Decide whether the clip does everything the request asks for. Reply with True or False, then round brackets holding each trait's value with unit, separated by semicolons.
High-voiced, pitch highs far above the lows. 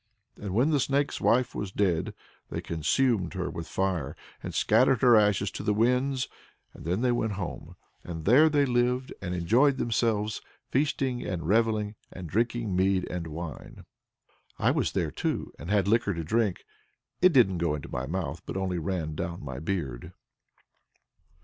False (100 Hz; 5.8 semitones)